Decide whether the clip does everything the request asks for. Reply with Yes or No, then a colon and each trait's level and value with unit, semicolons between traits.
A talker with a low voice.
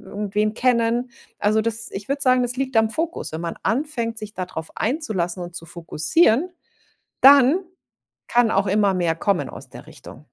No: high, 220 Hz